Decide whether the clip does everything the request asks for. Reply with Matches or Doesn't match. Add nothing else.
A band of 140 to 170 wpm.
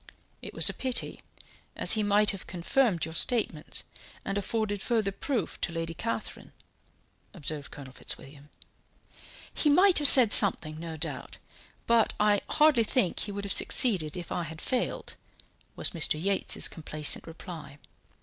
Matches